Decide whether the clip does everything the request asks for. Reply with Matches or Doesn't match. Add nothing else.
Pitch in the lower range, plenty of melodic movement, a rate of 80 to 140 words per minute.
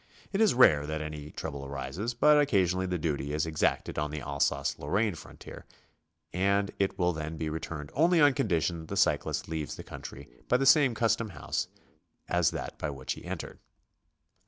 Doesn't match